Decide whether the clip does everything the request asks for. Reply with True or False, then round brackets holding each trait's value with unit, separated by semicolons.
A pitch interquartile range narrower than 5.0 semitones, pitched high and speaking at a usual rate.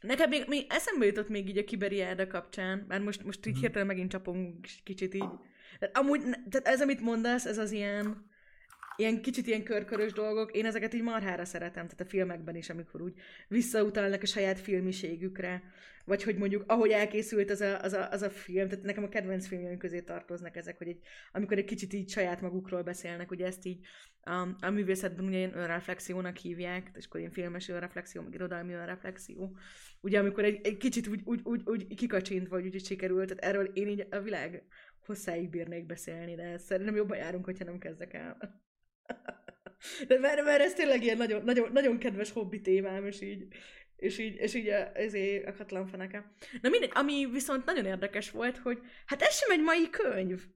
False (2.8 semitones; 200 Hz; 190 wpm)